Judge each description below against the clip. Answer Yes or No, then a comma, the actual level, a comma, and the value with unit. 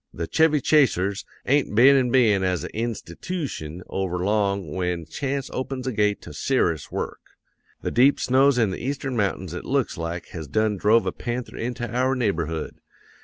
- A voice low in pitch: Yes, low, 110 Hz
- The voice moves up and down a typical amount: No, wide, 6.4 semitones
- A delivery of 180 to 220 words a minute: No, average, 170 wpm